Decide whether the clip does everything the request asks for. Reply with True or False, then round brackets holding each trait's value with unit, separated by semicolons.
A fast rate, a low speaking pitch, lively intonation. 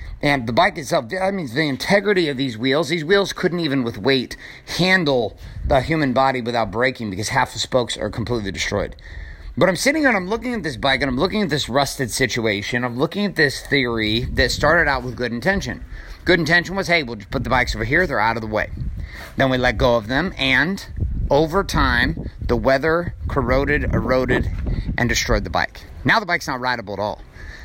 True (215 wpm; 130 Hz; 6.8 semitones)